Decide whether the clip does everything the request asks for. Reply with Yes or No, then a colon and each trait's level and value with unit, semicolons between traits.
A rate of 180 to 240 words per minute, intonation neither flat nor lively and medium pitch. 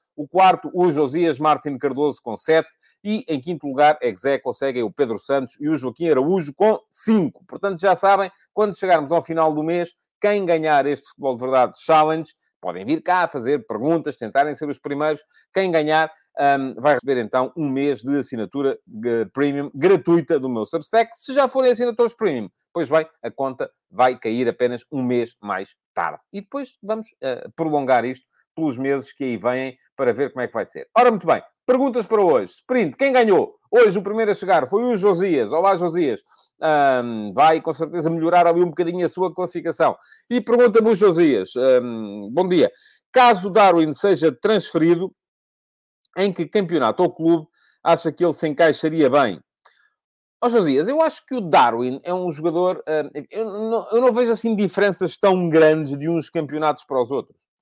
No: fast, 185 wpm; wide, 6.2 semitones; medium, 165 Hz